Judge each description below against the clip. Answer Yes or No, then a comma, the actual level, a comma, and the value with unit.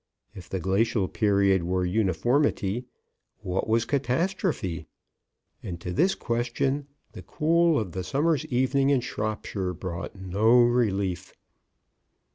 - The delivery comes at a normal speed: No, slow, 115 wpm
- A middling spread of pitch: No, wide, 6.2 semitones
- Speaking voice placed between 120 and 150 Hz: No, low, 110 Hz